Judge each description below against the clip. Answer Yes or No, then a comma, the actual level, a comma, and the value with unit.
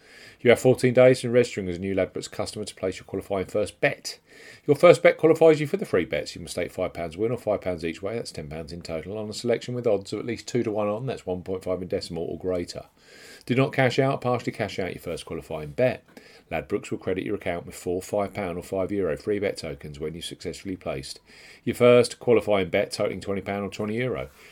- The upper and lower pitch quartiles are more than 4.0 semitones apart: Yes, average, 5.0 semitones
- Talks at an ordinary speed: No, fast, 255 wpm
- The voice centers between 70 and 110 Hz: Yes, low, 105 Hz